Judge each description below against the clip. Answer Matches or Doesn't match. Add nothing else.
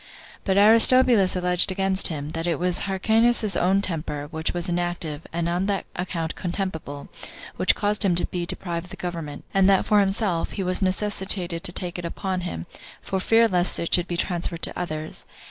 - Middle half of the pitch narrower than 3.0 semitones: Matches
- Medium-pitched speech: Matches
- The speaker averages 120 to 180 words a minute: Doesn't match